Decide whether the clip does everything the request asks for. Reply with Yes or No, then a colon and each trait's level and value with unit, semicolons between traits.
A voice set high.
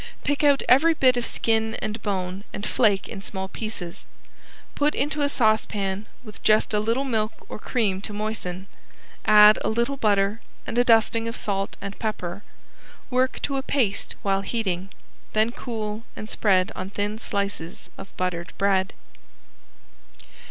Yes: high, 215 Hz